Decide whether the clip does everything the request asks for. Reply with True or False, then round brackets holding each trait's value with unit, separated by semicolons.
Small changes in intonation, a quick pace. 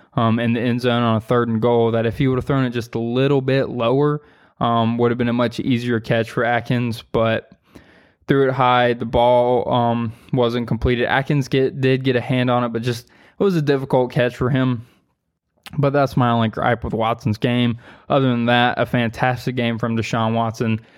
True (1.8 semitones; 215 wpm)